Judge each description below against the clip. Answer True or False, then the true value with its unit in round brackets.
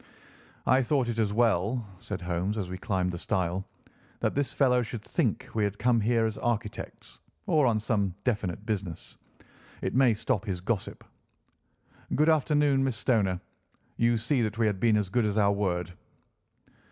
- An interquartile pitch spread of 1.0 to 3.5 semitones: False (3.9 semitones)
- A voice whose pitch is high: False (110 Hz)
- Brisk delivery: False (170 wpm)